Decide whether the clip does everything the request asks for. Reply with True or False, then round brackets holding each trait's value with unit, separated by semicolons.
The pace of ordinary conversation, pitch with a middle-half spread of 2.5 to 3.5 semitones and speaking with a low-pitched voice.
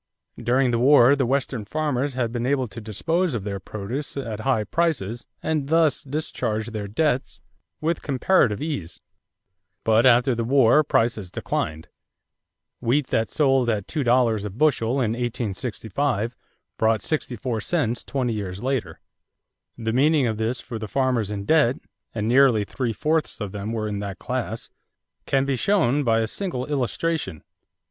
False (160 wpm; 4.1 semitones; 120 Hz)